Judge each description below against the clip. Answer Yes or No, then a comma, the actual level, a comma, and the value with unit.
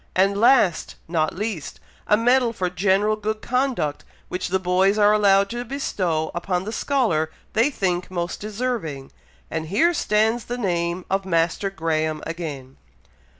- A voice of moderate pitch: No, high, 195 Hz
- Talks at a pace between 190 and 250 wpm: No, average, 150 wpm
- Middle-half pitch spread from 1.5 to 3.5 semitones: No, average, 4.3 semitones